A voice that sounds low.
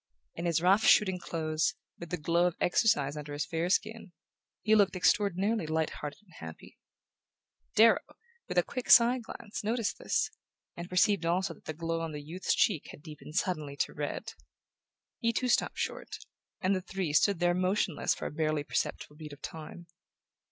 No: medium, 175 Hz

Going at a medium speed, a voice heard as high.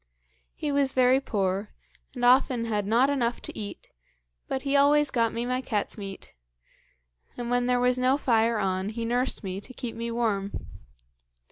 Yes: average, 170 wpm; high, 240 Hz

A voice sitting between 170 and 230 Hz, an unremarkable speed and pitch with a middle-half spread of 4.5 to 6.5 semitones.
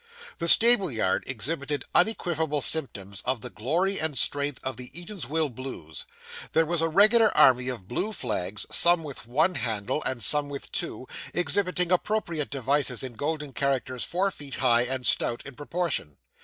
No: medium, 145 Hz; average, 160 wpm; average, 5.3 semitones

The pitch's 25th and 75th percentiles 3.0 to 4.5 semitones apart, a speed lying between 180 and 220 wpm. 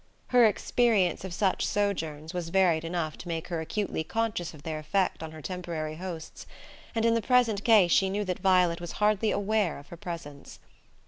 Yes: average, 4.2 semitones; average, 190 wpm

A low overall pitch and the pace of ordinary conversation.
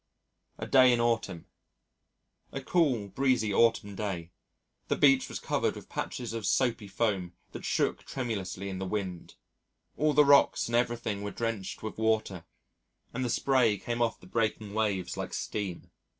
Yes: low, 110 Hz; average, 160 wpm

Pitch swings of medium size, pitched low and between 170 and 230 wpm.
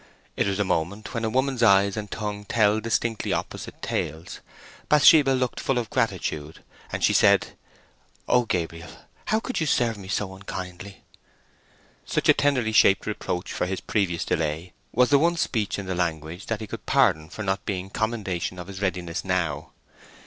Yes: average, 4.3 semitones; low, 100 Hz; average, 175 wpm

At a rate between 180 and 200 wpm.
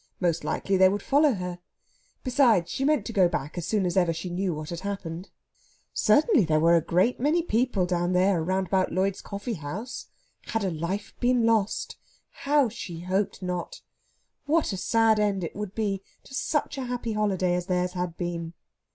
Yes: average, 185 wpm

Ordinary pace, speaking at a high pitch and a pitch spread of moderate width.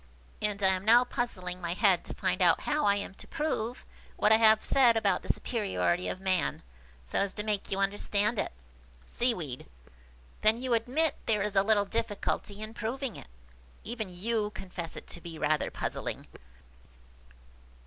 Yes: average, 170 wpm; high, 210 Hz; average, 3.4 semitones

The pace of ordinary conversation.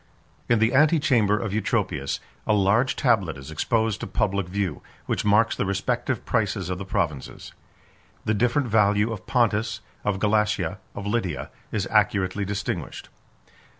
Yes: average, 145 wpm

